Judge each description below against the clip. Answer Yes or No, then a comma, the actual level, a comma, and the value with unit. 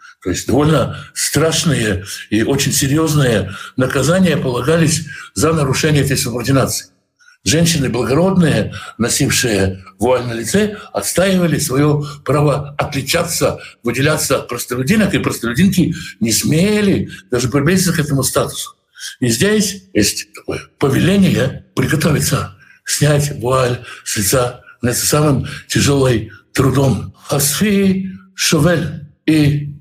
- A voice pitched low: No, medium, 145 Hz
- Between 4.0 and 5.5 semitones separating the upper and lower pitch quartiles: Yes, average, 4.8 semitones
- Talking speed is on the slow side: Yes, slow, 105 wpm